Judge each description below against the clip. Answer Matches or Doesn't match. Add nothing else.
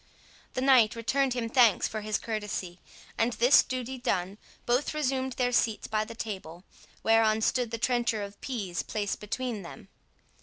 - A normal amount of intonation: Matches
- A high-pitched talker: Matches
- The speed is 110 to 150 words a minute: Doesn't match